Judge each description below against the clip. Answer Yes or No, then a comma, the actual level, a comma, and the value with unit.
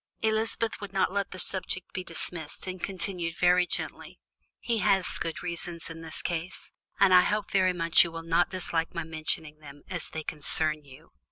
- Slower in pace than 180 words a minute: No, average, 185 wpm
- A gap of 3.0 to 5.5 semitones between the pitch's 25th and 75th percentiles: No, narrow, 2.4 semitones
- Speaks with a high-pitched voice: No, medium, 175 Hz